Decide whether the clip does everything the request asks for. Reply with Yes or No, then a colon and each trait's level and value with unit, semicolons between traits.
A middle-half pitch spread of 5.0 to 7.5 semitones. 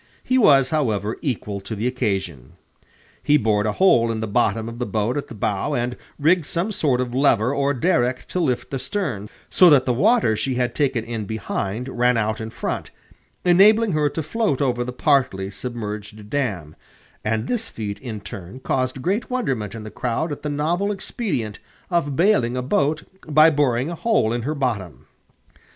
Yes: wide, 5.5 semitones